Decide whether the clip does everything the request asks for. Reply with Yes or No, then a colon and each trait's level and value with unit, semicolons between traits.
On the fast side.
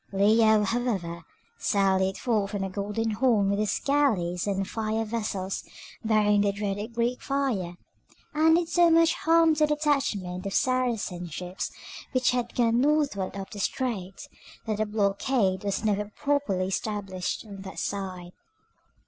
No: average, 150 wpm